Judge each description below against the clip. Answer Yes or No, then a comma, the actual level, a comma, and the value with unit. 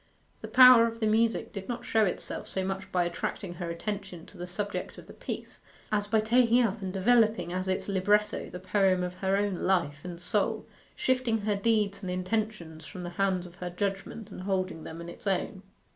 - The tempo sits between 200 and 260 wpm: Yes, fast, 205 wpm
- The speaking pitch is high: Yes, high, 195 Hz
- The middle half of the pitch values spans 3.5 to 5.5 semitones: No, average, 3.1 semitones